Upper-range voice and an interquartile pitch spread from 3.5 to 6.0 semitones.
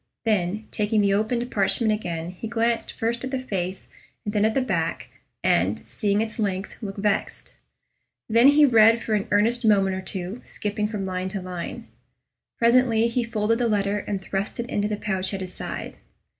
No: high, 210 Hz; average, 2.9 semitones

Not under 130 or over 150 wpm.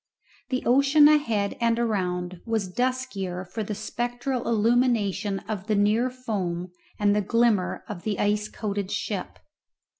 Yes: average, 145 wpm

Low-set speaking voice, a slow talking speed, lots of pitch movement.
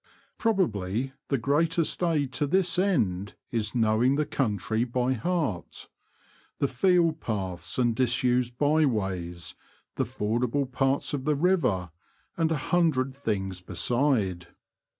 Yes: low, 130 Hz; slow, 125 wpm; wide, 6.2 semitones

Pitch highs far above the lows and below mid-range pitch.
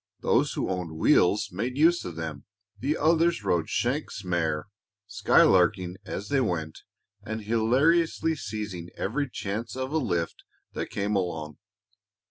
Yes: wide, 7.0 semitones; low, 105 Hz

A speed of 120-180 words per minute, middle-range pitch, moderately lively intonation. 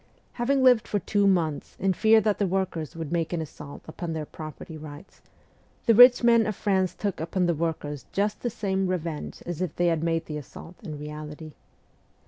No: average, 195 wpm; medium, 175 Hz; average, 4.5 semitones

